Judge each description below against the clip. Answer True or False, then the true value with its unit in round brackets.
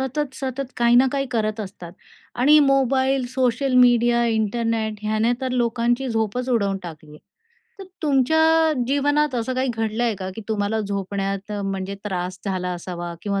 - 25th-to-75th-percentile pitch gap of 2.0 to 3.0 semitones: False (4.6 semitones)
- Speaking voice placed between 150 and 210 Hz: False (230 Hz)